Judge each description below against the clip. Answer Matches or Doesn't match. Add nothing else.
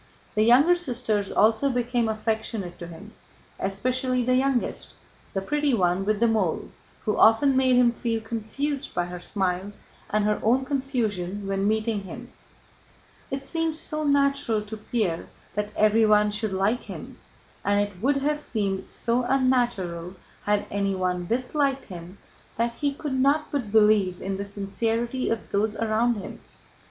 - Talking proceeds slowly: Doesn't match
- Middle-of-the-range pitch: Doesn't match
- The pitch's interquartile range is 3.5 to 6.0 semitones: Matches